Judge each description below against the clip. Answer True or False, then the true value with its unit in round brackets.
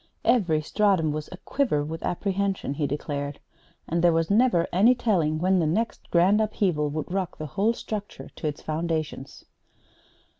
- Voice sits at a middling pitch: True (170 Hz)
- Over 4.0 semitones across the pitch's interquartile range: True (4.5 semitones)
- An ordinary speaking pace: True (155 wpm)